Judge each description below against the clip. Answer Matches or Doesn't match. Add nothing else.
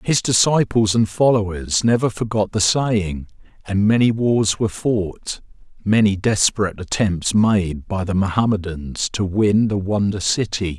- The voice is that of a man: Matches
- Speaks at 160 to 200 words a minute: Doesn't match